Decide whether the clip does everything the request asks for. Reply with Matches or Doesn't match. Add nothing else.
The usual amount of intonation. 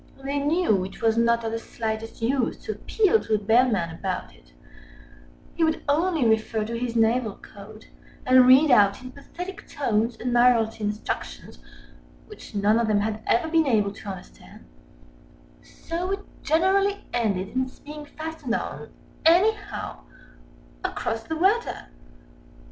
Doesn't match